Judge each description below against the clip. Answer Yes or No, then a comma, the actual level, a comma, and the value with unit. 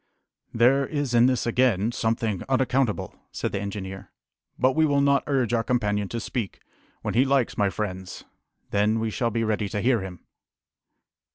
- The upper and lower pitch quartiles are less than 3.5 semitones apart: No, average, 4.0 semitones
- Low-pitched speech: Yes, low, 115 Hz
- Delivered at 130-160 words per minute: No, average, 170 wpm